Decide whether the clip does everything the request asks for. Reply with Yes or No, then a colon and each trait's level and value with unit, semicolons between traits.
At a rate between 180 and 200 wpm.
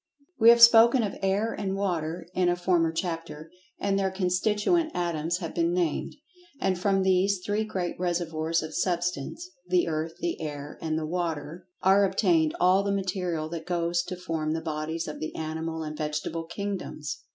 No: average, 165 wpm